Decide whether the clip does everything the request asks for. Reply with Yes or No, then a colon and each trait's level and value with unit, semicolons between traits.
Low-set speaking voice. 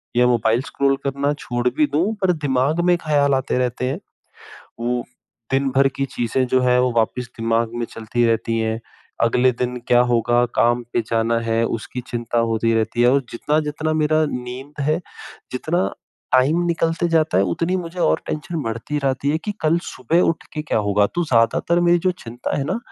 Yes: low, 125 Hz